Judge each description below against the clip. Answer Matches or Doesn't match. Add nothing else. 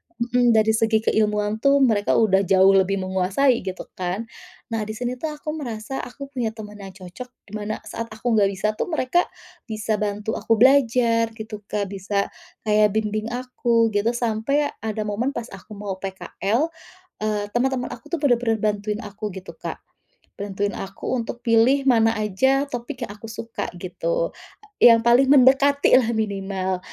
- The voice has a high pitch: Matches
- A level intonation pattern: Doesn't match